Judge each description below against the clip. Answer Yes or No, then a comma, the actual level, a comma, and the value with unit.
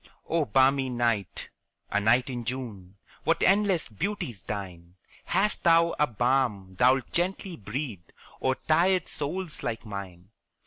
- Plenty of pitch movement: Yes, wide, 8.2 semitones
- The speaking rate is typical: No, slow, 130 wpm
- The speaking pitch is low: Yes, low, 130 Hz